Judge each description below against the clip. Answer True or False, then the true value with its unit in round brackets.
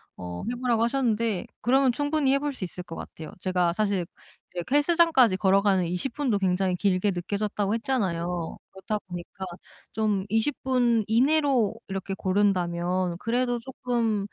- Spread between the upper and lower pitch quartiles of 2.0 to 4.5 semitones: False (5.1 semitones)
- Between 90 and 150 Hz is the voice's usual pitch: False (210 Hz)